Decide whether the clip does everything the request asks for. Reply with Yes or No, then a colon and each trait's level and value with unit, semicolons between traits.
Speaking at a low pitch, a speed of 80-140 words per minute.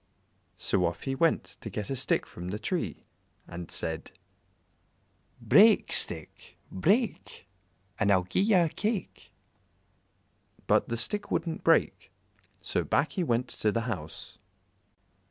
Yes: low, 115 Hz; slow, 135 wpm